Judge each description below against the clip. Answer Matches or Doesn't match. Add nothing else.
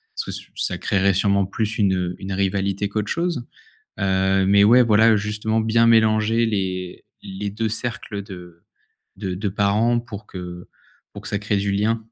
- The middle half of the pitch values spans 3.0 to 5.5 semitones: Doesn't match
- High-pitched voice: Doesn't match